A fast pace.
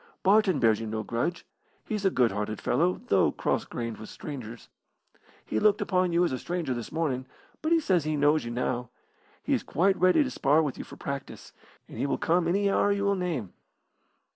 Yes: fast, 210 wpm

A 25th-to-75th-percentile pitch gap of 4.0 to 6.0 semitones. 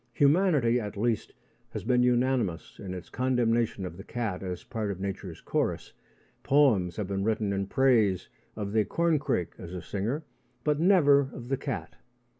Yes: wide, 5.4 semitones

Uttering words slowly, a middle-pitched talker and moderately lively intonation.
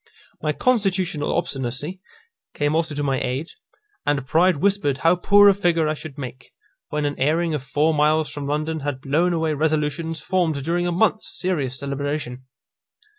No: average, 165 wpm; medium, 155 Hz; average, 3.2 semitones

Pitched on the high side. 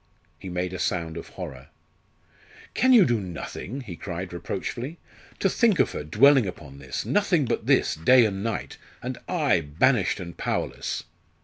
No: very low, 95 Hz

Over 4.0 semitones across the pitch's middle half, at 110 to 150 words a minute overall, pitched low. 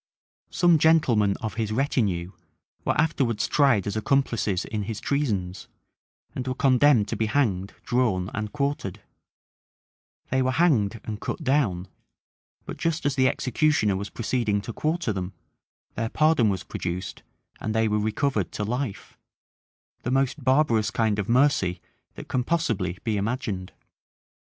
Yes: average, 5.1 semitones; average, 145 wpm; low, 115 Hz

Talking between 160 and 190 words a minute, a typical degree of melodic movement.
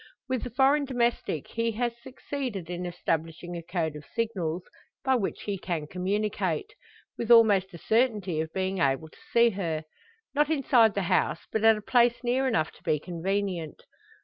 No: average, 175 wpm; wide, 5.7 semitones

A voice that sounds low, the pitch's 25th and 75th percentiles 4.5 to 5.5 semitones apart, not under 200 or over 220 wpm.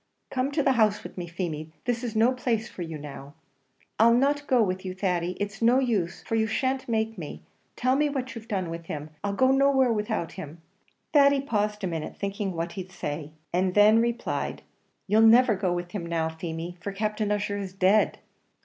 No: high, 205 Hz; average, 5.2 semitones; fast, 205 wpm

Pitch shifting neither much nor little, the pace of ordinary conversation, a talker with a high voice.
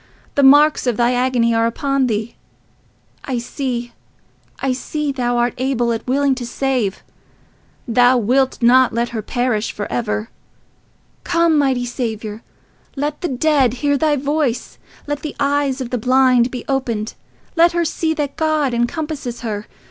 Yes: average, 3.2 semitones; average, 150 wpm; very high, 255 Hz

